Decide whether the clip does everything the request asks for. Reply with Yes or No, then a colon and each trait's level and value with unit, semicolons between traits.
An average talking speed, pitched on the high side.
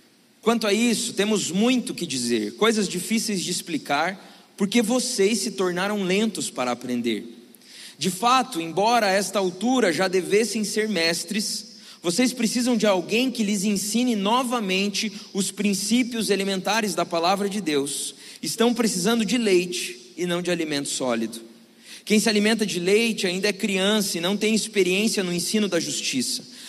Yes: average, 155 wpm; high, 205 Hz